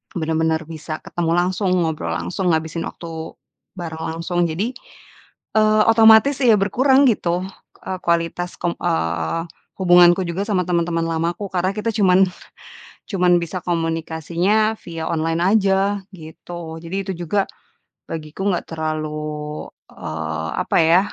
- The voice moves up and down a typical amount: Yes, average, 3.0 semitones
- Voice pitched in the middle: Yes, medium, 170 Hz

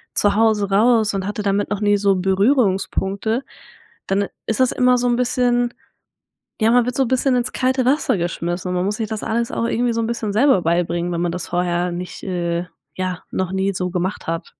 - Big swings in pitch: No, average, 4.6 semitones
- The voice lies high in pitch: Yes, high, 205 Hz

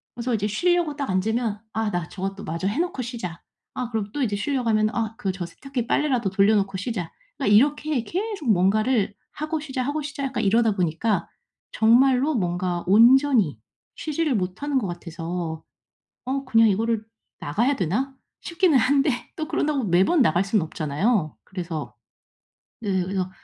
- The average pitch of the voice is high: Yes, high, 220 Hz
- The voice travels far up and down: Yes, wide, 6.3 semitones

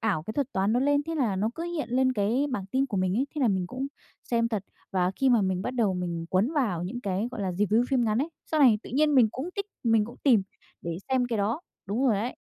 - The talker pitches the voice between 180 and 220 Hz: No, high, 230 Hz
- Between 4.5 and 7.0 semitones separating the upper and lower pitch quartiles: Yes, average, 5.2 semitones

